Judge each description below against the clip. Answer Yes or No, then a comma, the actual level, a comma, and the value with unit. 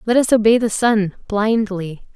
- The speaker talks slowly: No, average, 165 wpm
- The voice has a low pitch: No, high, 215 Hz